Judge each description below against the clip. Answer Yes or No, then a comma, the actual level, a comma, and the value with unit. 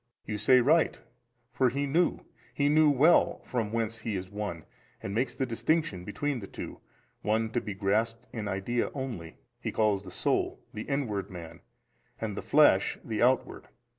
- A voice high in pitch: No, low, 115 Hz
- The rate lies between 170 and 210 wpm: Yes, average, 175 wpm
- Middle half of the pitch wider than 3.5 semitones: Yes, average, 4.7 semitones